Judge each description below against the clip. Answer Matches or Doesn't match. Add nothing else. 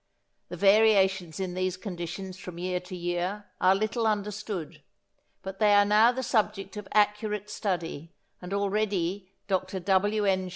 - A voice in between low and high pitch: Doesn't match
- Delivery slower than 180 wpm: Matches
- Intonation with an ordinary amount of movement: Doesn't match